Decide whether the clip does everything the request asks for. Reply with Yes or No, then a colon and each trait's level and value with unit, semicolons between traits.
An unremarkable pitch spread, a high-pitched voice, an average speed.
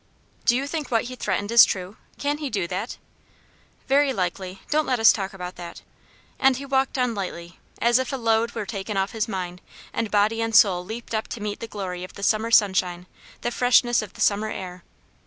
No: average, 4.0 semitones; high, 220 Hz; fast, 210 wpm